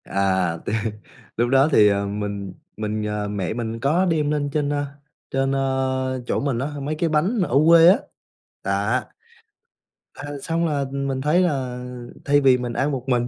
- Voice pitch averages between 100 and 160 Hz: Yes, low, 135 Hz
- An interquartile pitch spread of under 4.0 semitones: No, wide, 5.5 semitones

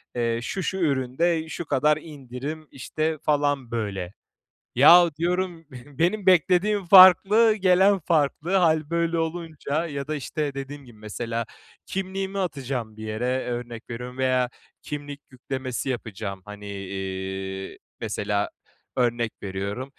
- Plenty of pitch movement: Yes, wide, 6.1 semitones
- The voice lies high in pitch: No, medium, 140 Hz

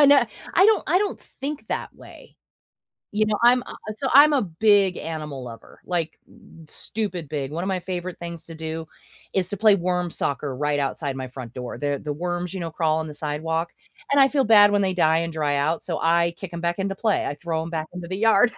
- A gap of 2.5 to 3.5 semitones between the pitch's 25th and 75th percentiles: No, average, 4.5 semitones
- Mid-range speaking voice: Yes, medium, 170 Hz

